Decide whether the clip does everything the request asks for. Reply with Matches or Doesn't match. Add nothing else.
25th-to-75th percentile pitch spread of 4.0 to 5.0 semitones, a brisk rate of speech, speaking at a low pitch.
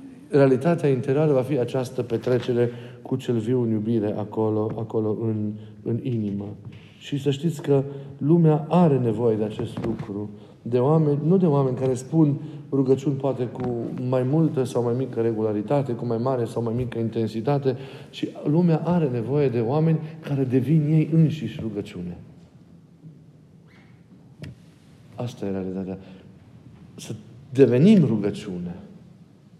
Doesn't match